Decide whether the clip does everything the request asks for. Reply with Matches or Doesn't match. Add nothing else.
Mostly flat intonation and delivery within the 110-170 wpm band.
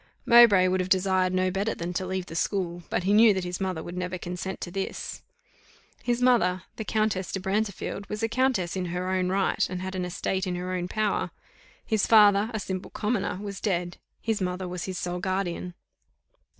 Doesn't match